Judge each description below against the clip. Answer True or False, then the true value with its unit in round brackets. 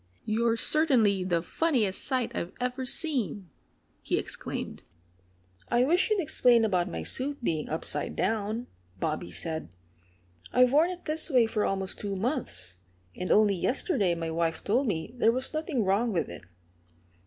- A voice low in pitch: False (225 Hz)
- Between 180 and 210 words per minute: False (155 wpm)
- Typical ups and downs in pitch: False (5.9 semitones)